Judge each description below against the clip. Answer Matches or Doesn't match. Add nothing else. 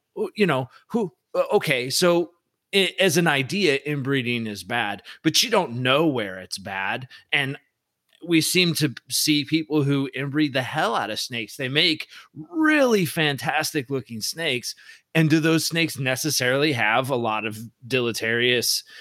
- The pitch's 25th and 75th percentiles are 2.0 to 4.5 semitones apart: Doesn't match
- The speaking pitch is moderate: Matches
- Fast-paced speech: Doesn't match